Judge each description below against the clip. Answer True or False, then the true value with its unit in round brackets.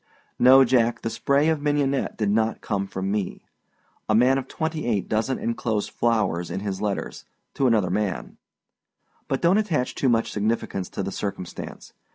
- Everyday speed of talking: True (170 wpm)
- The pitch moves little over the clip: False (4.7 semitones)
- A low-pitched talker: True (115 Hz)